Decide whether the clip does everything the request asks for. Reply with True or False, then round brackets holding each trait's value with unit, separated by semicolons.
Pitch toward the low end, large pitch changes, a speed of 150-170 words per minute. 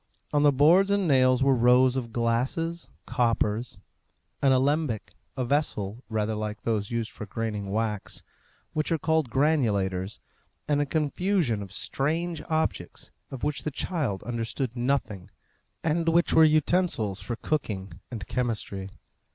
False (130 Hz; 5.8 semitones; 140 wpm)